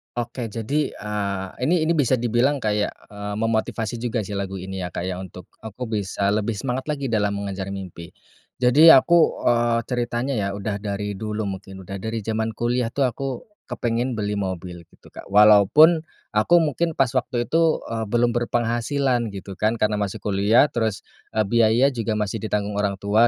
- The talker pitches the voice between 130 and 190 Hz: No, low, 110 Hz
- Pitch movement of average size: Yes, average, 3.1 semitones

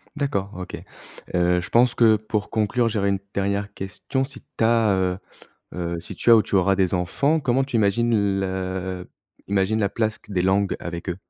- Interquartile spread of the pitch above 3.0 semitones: Yes, average, 3.5 semitones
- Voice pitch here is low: Yes, low, 100 Hz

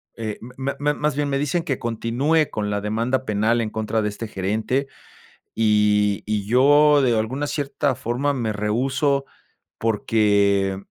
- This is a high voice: No, low, 115 Hz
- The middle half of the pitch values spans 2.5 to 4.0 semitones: No, average, 4.7 semitones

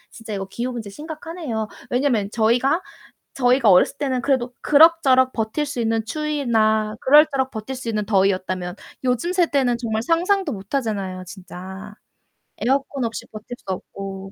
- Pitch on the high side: Yes, high, 235 Hz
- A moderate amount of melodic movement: Yes, average, 4.8 semitones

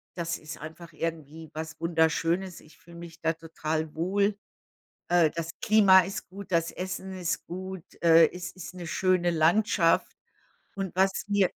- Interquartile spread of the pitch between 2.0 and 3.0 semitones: Yes, narrow, 2.6 semitones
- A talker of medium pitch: Yes, medium, 170 Hz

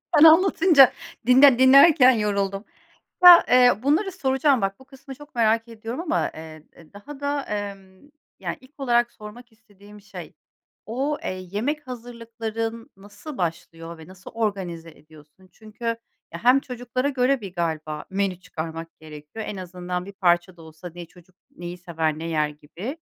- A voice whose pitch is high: Yes, high, 210 Hz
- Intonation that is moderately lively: No, wide, 6.7 semitones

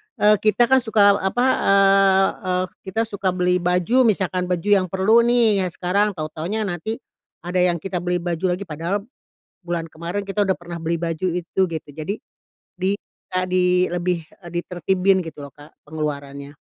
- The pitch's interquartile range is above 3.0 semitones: No, average, 2.7 semitones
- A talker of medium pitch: Yes, medium, 180 Hz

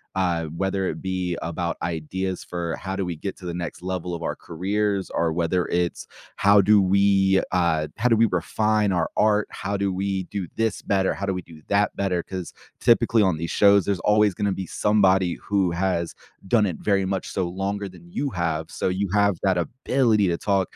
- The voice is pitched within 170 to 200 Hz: No, very low, 95 Hz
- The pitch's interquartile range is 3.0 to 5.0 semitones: No, narrow, 2.6 semitones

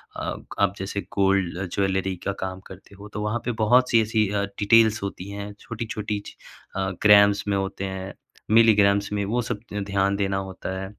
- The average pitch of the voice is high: No, low, 100 Hz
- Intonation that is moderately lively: No, narrow, 1.6 semitones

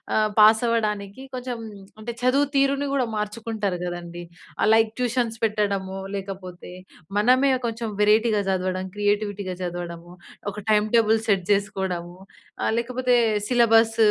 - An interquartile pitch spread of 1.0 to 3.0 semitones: No, average, 3.5 semitones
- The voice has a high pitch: Yes, high, 210 Hz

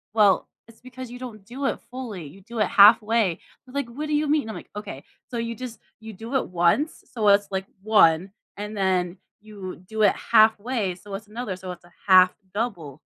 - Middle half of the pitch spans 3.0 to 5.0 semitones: Yes, average, 4.0 semitones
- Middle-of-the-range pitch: No, high, 215 Hz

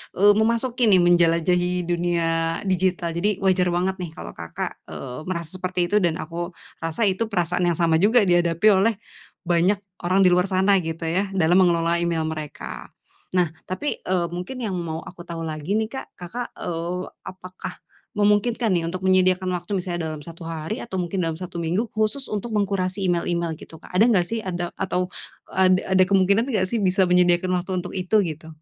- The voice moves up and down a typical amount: No, narrow, 2.3 semitones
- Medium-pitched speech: Yes, medium, 180 Hz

